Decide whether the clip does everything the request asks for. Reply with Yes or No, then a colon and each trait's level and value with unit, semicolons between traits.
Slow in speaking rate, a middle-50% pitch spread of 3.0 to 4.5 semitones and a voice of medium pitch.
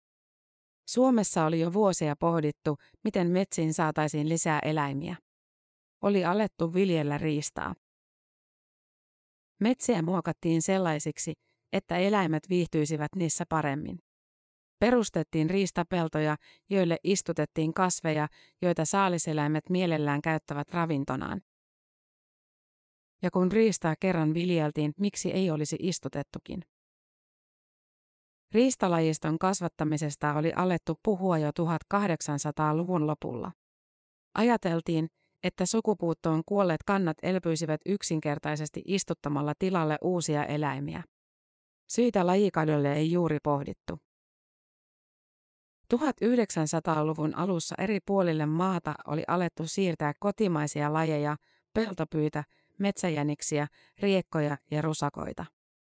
Yes: slow, 85 wpm; average, 3.5 semitones; medium, 165 Hz